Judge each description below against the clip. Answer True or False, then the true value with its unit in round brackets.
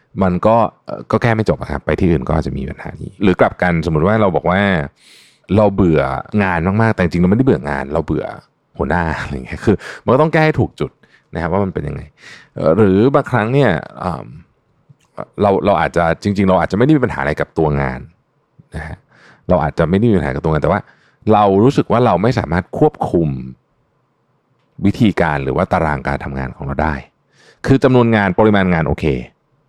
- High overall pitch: False (95 Hz)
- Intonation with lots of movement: True (6.1 semitones)